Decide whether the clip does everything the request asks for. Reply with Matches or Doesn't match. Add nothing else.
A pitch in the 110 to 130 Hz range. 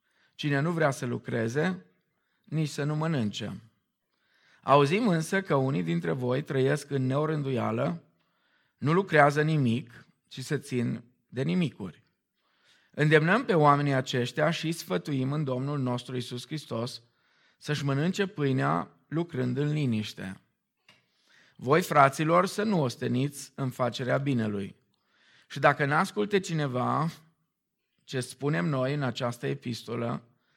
Doesn't match